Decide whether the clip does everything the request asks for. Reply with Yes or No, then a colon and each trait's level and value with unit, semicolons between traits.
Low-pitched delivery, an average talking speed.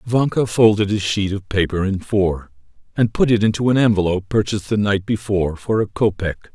Yes: low, 100 Hz; average, 190 wpm